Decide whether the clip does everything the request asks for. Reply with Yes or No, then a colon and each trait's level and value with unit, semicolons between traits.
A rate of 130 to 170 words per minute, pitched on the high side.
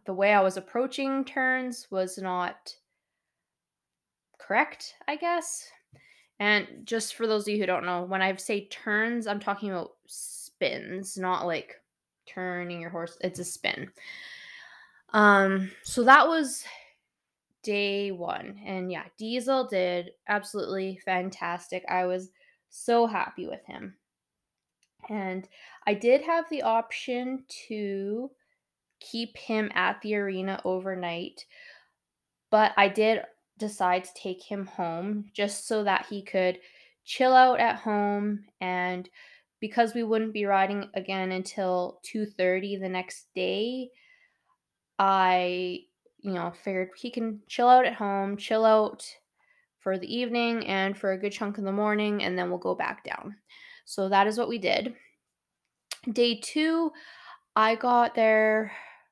Yes: average, 140 wpm; high, 205 Hz